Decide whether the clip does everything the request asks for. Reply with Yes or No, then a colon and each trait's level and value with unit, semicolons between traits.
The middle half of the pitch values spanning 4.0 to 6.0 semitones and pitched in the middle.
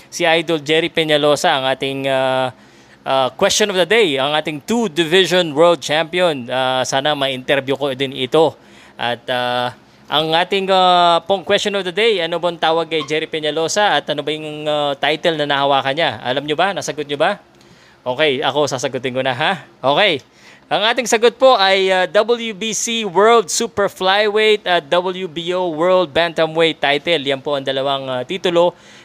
Yes: average, 5.1 semitones; medium, 160 Hz